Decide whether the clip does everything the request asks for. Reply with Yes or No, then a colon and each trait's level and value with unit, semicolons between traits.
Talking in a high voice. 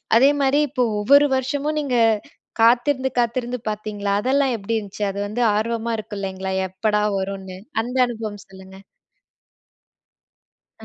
Yes: high, 225 Hz